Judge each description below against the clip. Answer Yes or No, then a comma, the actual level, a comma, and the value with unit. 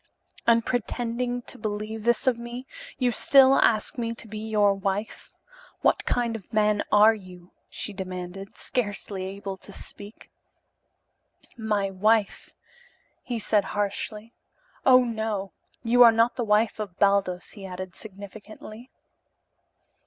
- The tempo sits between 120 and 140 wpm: Yes, slow, 135 wpm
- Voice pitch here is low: No, high, 215 Hz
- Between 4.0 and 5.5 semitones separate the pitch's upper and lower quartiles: No, average, 2.7 semitones